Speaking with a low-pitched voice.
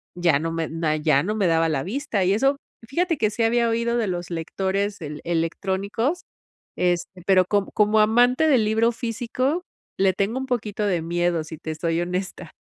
No: high, 200 Hz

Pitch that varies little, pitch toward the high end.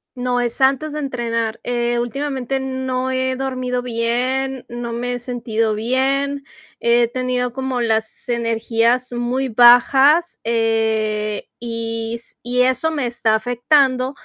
Yes: narrow, 2.1 semitones; high, 245 Hz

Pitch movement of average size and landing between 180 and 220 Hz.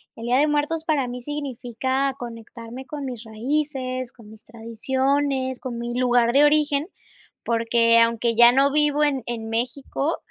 No: average, 3.4 semitones; very high, 255 Hz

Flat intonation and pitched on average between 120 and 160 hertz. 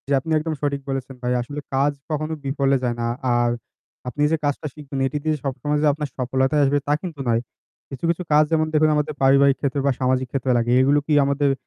Yes: narrow, 2.2 semitones; medium, 140 Hz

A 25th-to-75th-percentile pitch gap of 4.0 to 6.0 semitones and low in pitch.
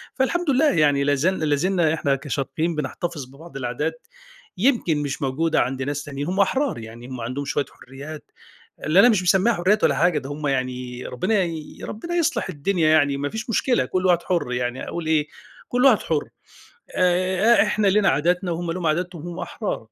No: average, 5.1 semitones; medium, 165 Hz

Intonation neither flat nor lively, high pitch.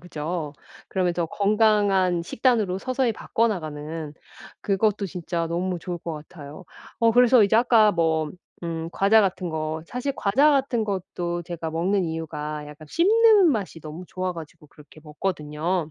No: average, 5.0 semitones; medium, 180 Hz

